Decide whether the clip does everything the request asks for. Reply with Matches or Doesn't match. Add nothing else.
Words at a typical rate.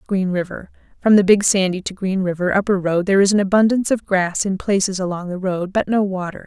Doesn't match